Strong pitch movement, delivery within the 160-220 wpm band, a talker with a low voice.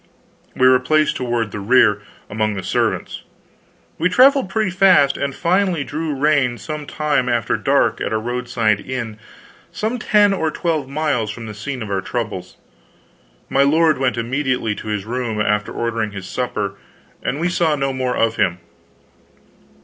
Yes: wide, 5.8 semitones; average, 165 wpm; low, 130 Hz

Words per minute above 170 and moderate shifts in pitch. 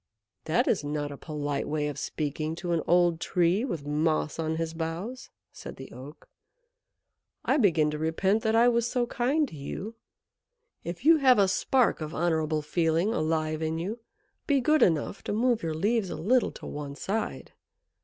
No: average, 180 wpm; wide, 6.3 semitones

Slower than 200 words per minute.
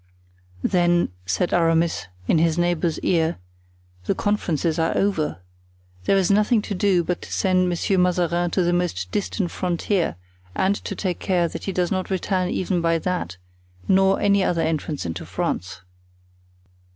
Yes: average, 155 wpm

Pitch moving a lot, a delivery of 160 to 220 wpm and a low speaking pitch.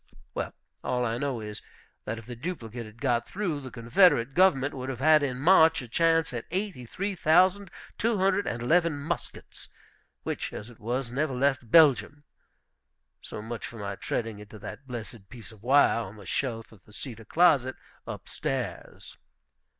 Yes: wide, 5.8 semitones; average, 175 wpm; low, 130 Hz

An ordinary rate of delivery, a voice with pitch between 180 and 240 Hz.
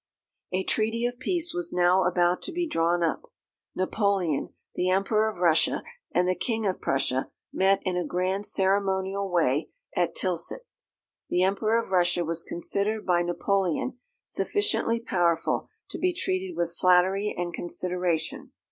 Yes: average, 145 wpm; medium, 185 Hz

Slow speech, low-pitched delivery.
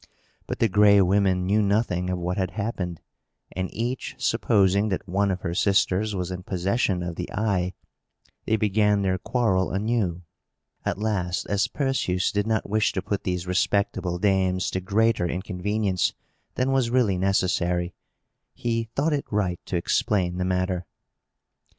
No: average, 155 wpm; very low, 95 Hz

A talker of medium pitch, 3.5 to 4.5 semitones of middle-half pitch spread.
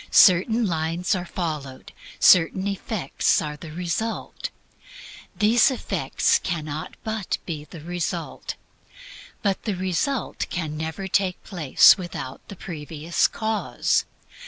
Yes: medium, 175 Hz; average, 4.0 semitones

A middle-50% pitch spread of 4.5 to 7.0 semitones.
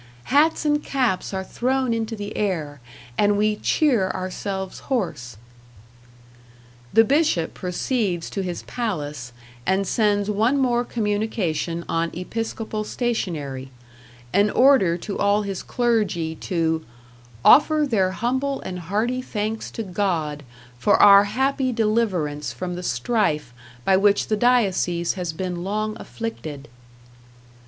Yes: average, 4.9 semitones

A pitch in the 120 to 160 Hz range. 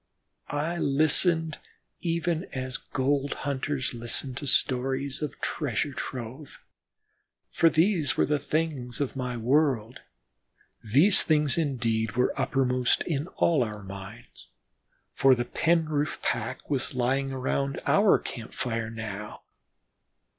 Yes: low, 135 Hz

